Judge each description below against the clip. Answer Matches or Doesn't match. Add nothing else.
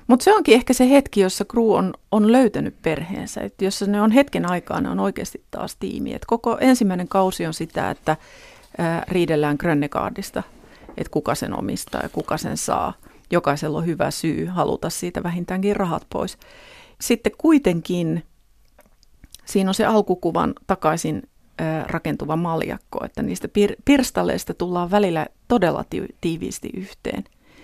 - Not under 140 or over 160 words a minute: Matches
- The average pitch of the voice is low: Doesn't match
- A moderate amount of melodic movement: Doesn't match